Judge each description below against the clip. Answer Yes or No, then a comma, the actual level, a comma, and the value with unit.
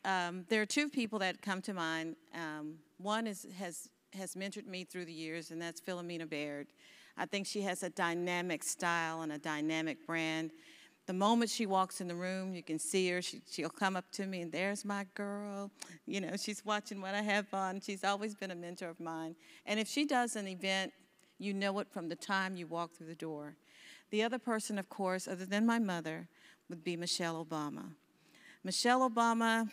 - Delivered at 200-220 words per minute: Yes, fast, 205 wpm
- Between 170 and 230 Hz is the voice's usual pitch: Yes, medium, 185 Hz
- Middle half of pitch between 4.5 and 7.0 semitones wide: No, average, 3.4 semitones